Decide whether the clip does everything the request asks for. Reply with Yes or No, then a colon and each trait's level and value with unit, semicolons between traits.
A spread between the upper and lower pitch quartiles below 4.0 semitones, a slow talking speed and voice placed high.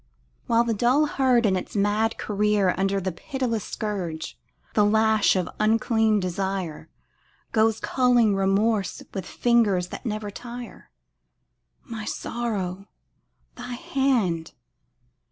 Yes: average, 3.3 semitones; slow, 115 wpm; high, 215 Hz